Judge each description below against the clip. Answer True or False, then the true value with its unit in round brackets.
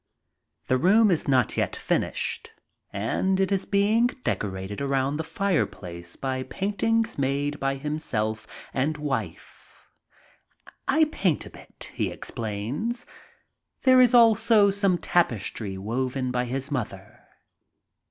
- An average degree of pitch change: False (8.7 semitones)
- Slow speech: True (120 wpm)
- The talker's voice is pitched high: False (140 Hz)